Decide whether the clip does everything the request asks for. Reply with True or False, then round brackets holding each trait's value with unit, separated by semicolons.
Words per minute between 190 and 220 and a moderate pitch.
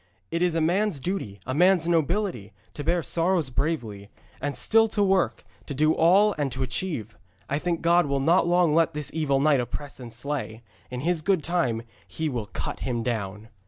True (195 wpm; 155 Hz)